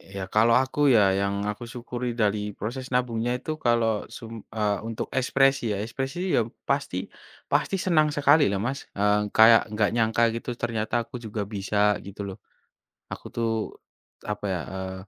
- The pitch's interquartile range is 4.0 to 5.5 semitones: No, average, 3.5 semitones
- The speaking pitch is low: Yes, low, 115 Hz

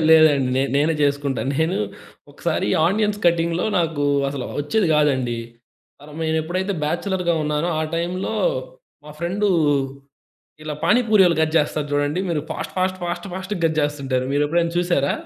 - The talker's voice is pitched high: No, medium, 160 Hz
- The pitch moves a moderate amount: Yes, average, 3.3 semitones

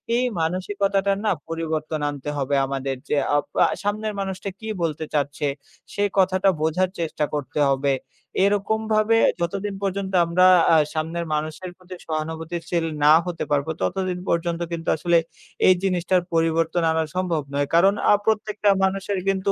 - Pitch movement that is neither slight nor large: Yes, average, 3.7 semitones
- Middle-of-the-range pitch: Yes, medium, 175 Hz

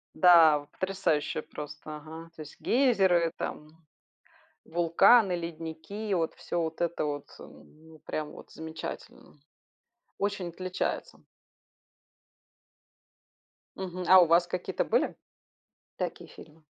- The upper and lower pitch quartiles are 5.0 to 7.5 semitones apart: No, average, 2.7 semitones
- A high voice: No, medium, 165 Hz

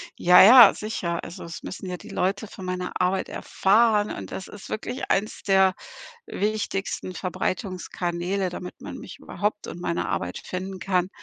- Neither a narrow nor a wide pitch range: No, narrow, 2.3 semitones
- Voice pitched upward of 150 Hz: Yes, high, 190 Hz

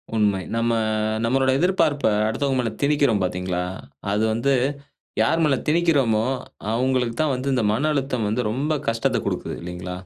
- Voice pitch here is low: Yes, low, 125 Hz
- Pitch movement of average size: Yes, average, 4.5 semitones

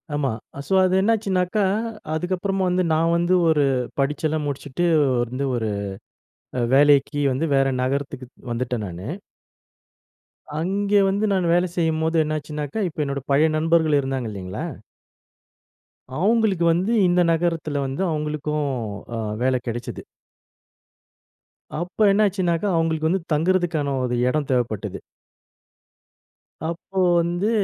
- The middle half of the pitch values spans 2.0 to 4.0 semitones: No, average, 4.5 semitones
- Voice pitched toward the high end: No, medium, 160 Hz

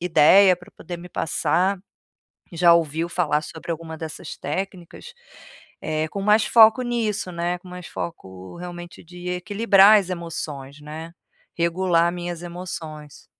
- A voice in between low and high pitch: Yes, medium, 175 Hz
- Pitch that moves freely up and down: No, narrow, 2.5 semitones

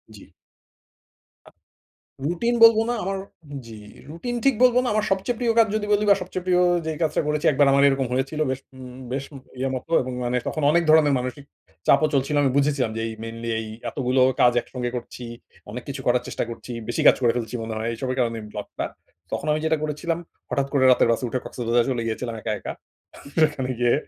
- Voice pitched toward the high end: No, low, 135 Hz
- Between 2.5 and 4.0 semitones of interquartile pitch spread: No, average, 4.6 semitones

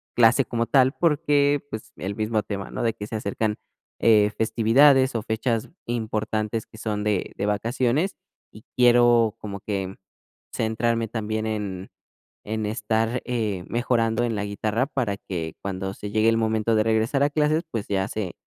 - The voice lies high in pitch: No, low, 110 Hz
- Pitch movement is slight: Yes, narrow, 2.3 semitones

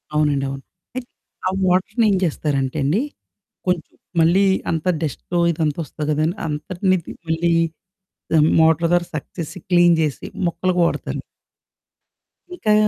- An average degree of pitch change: Yes, average, 3.0 semitones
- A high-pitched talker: No, medium, 165 Hz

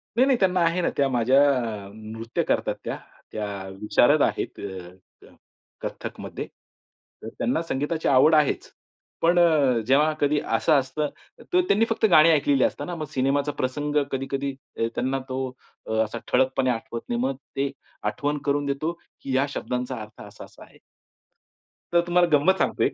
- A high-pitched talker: No, medium, 140 Hz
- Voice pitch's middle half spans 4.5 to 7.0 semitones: No, average, 3.8 semitones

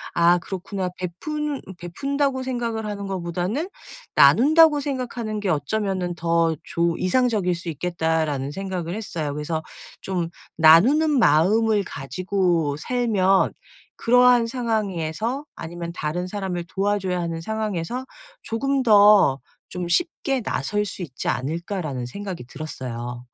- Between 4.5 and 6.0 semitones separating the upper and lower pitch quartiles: Yes, average, 5.3 semitones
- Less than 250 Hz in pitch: Yes, medium, 185 Hz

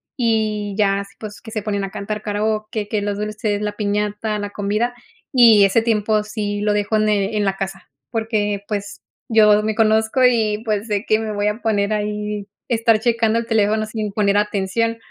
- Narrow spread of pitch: Yes, narrow, 1.2 semitones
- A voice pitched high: Yes, high, 210 Hz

